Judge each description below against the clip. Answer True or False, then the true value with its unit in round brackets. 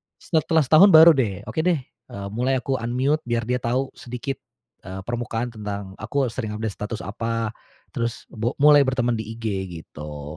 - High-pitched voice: False (120 Hz)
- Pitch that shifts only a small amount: False (3.7 semitones)